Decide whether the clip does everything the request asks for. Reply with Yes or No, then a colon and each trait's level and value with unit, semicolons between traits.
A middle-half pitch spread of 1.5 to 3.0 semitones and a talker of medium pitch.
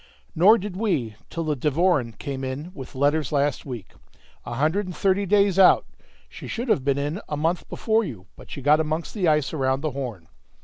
No: average, 5.3 semitones; medium, 150 Hz